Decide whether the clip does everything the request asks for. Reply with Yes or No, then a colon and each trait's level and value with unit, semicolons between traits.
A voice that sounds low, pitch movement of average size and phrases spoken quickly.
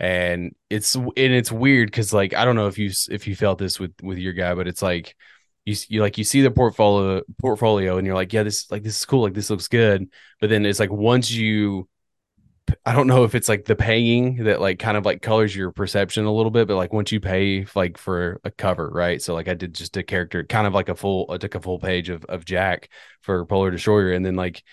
Yes: low, 100 Hz; average, 3.0 semitones; fast, 255 wpm